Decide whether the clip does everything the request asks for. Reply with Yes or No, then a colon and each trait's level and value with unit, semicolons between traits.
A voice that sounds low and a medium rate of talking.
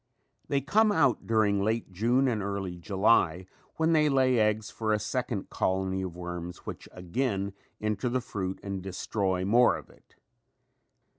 Yes: low, 105 Hz; average, 155 wpm